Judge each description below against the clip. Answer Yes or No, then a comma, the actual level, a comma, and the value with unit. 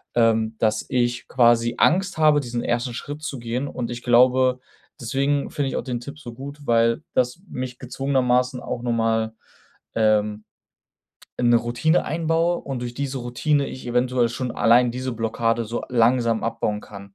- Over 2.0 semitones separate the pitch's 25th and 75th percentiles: Yes, narrow, 2.4 semitones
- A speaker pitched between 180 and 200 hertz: No, low, 120 Hz